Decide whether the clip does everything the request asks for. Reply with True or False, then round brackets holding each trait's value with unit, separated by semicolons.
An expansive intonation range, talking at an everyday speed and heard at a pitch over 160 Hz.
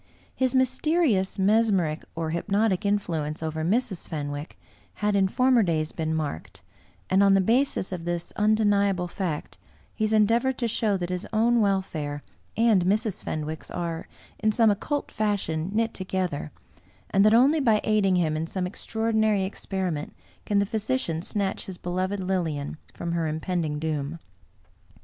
False (4.6 semitones; 155 wpm; 190 Hz)